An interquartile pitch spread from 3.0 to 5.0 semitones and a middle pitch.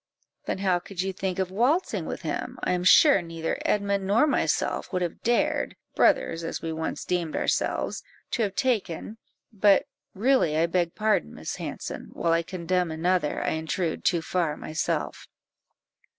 Yes: average, 3.4 semitones; medium, 180 Hz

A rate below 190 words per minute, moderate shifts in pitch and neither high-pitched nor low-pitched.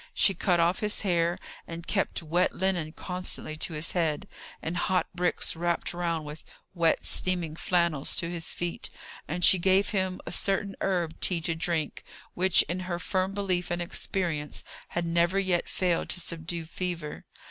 No: average, 170 wpm; narrow, 1.7 semitones; medium, 175 Hz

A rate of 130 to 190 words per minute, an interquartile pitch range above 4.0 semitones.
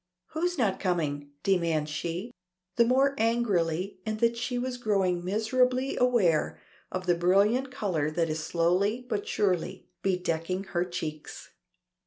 Yes: slow, 135 wpm; wide, 5.6 semitones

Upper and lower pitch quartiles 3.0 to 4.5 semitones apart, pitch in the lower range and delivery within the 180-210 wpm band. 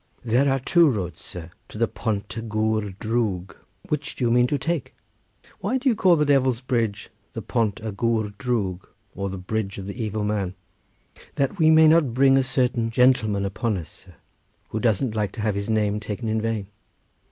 Yes: average, 4.0 semitones; low, 110 Hz; average, 200 wpm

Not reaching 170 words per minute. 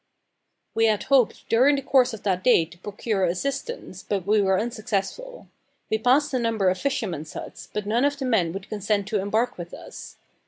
No: average, 195 wpm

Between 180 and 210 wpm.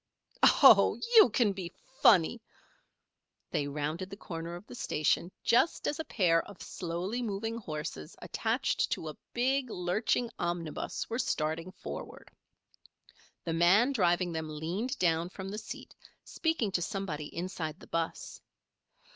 No: average, 140 wpm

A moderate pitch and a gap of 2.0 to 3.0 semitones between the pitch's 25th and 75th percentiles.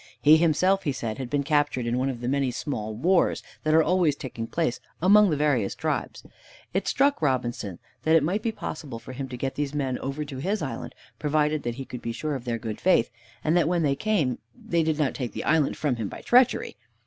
No: medium, 145 Hz; average, 4.4 semitones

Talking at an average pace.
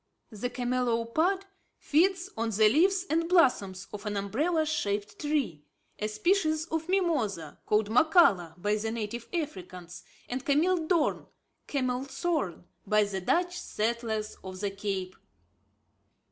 No: slow, 125 wpm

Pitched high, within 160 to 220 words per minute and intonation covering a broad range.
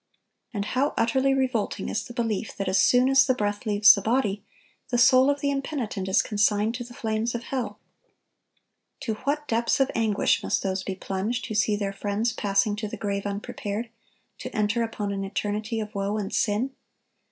No: high, 220 Hz; average, 190 wpm; average, 3.1 semitones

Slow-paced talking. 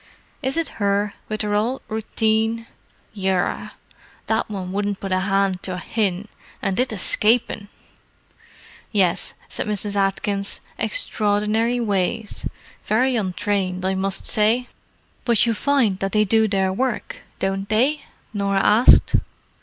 Yes: slow, 130 wpm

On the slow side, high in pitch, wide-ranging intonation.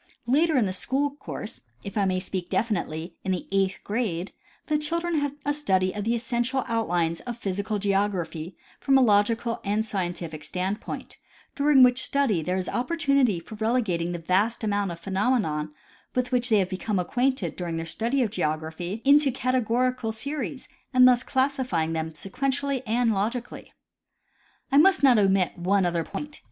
No: average, 165 wpm; high, 220 Hz; wide, 5.7 semitones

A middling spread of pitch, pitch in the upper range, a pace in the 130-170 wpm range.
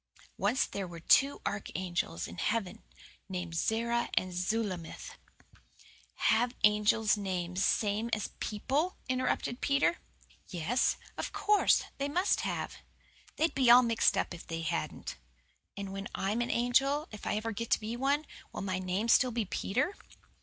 Yes: average, 4.7 semitones; high, 215 Hz; average, 155 wpm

